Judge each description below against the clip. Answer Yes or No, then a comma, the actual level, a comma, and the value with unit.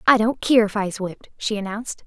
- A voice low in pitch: No, high, 215 Hz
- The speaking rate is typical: No, fast, 260 wpm